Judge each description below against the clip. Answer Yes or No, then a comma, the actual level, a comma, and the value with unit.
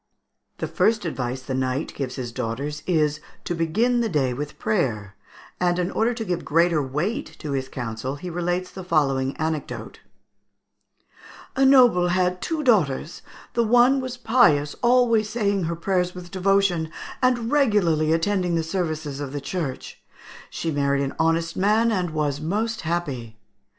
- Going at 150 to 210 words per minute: Yes, average, 160 wpm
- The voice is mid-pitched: Yes, medium, 170 Hz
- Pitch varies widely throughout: Yes, wide, 6.2 semitones